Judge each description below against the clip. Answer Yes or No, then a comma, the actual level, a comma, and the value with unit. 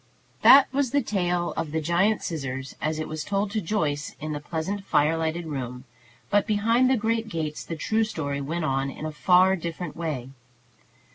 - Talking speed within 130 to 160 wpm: No, average, 190 wpm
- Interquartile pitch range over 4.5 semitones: Yes, average, 5.2 semitones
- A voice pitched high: No, medium, 165 Hz